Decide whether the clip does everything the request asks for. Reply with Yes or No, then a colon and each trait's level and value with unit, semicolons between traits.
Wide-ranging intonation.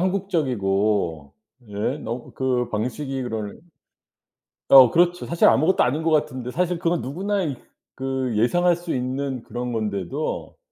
Yes: wide, 6.6 semitones